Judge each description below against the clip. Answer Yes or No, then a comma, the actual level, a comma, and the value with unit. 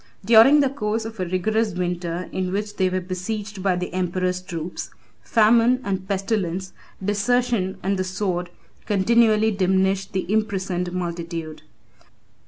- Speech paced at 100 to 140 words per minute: Yes, slow, 135 wpm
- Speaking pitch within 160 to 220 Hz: Yes, high, 190 Hz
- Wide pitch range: No, average, 2.9 semitones